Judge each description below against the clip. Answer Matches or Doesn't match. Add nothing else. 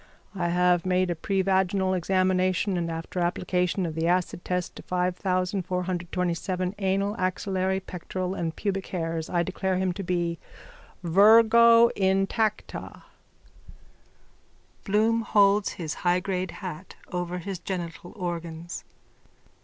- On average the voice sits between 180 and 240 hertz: Matches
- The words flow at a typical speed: Doesn't match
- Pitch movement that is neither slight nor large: Doesn't match